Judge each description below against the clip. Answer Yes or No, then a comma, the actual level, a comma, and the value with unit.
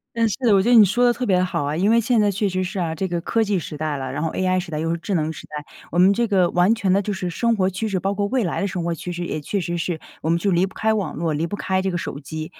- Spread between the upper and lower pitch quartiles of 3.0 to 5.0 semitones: Yes, average, 3.6 semitones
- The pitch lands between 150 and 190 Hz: Yes, medium, 185 Hz